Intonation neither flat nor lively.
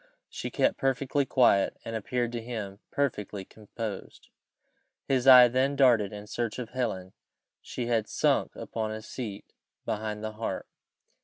Yes: average, 3.1 semitones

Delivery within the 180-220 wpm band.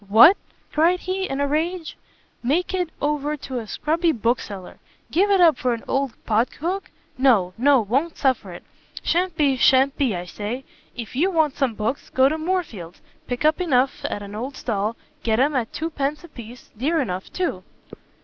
Yes: average, 190 wpm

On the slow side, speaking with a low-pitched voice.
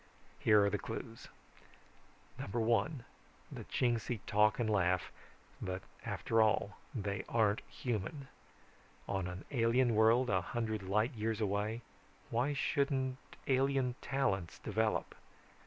Yes: slow, 115 wpm; low, 110 Hz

